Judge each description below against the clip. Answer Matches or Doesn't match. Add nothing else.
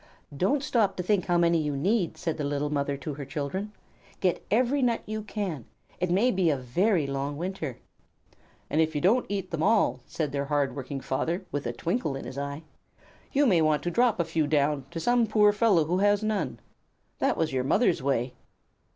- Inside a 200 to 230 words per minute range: Matches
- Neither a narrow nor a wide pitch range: Doesn't match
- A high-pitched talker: Doesn't match